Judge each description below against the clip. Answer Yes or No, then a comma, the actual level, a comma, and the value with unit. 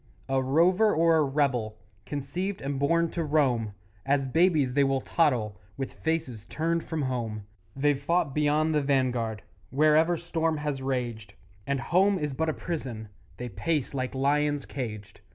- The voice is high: No, medium, 140 Hz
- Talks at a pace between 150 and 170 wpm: Yes, average, 155 wpm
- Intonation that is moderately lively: Yes, average, 3.9 semitones